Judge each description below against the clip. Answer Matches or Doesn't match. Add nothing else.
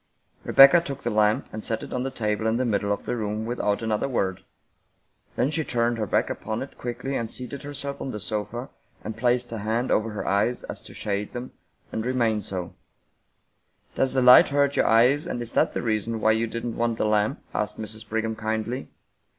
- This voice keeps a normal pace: Doesn't match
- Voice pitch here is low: Matches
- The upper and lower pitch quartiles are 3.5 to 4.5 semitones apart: Doesn't match